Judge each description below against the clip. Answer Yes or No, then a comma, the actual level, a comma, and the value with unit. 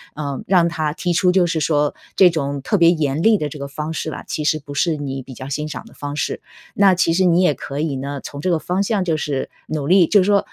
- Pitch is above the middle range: No, medium, 155 Hz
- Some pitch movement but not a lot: Yes, average, 4.0 semitones